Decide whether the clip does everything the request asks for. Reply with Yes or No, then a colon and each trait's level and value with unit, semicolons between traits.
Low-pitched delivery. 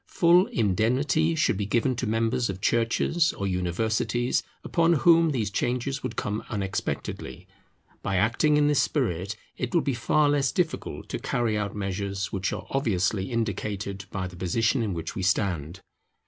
Yes: low, 110 Hz